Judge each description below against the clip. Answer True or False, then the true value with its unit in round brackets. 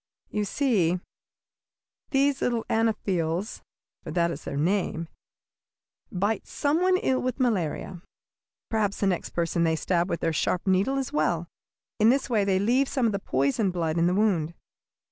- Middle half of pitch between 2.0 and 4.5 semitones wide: False (5.3 semitones)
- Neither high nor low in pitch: False (195 Hz)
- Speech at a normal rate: True (165 wpm)